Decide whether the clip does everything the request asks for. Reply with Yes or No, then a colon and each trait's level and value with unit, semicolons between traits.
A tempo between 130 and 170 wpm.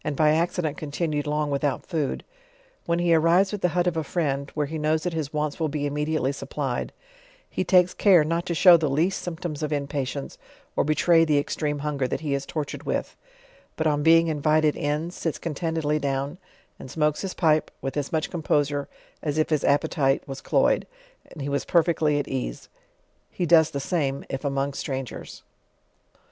No: average, 185 wpm